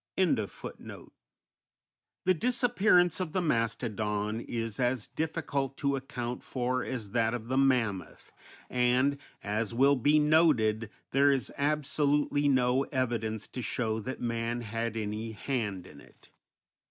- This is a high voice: No, low, 125 Hz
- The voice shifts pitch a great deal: No, average, 4.1 semitones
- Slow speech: Yes, slow, 130 wpm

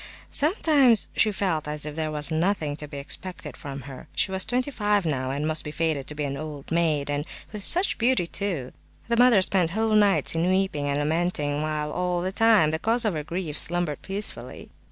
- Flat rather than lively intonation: No, average, 5.3 semitones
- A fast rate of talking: Yes, fast, 210 wpm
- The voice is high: No, medium, 165 Hz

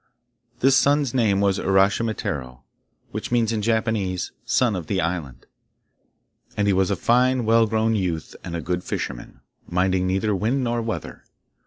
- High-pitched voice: No, low, 100 Hz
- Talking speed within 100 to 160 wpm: Yes, average, 155 wpm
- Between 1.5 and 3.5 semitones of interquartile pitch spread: No, average, 4.0 semitones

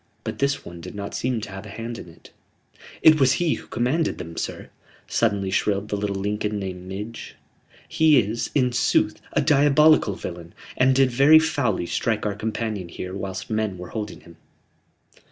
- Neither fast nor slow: Yes, average, 180 wpm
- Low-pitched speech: Yes, low, 105 Hz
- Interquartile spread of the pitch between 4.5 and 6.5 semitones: Yes, average, 5.1 semitones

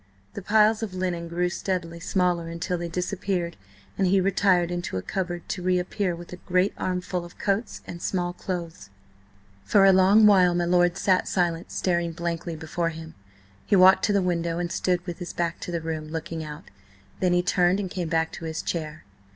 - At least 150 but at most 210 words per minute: Yes, average, 195 wpm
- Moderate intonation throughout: No, narrow, 1.7 semitones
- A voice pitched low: No, medium, 175 Hz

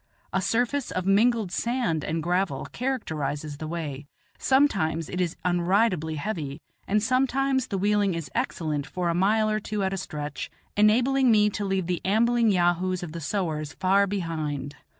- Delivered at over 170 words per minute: No, average, 165 wpm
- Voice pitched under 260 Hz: Yes, medium, 185 Hz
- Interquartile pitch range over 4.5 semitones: Yes, average, 5.2 semitones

